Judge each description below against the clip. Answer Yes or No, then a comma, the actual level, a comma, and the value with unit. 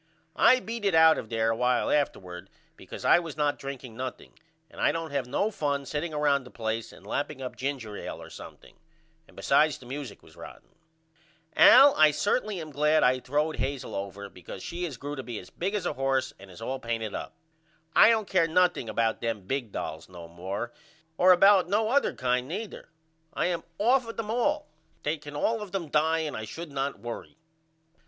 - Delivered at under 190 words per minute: No, fast, 205 wpm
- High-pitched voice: No, medium, 145 Hz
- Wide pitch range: Yes, wide, 6.6 semitones